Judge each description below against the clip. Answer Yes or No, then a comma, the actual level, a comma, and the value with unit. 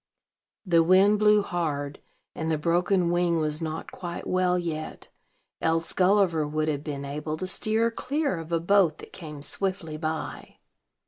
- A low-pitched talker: No, medium, 170 Hz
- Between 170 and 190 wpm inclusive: No, average, 155 wpm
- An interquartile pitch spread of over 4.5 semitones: No, average, 3.2 semitones